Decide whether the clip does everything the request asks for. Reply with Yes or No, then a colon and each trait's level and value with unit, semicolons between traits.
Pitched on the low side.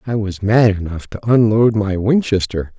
Yes: low, 105 Hz